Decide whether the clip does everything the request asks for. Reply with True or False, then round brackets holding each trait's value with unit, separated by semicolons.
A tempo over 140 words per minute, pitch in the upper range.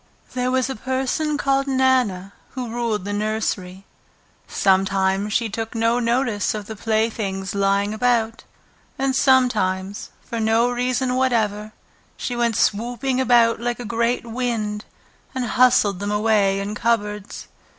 False (135 wpm; 225 Hz)